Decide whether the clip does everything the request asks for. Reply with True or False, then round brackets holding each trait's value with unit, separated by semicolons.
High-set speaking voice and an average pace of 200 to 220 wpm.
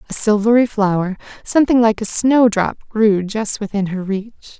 False (215 Hz; 170 wpm)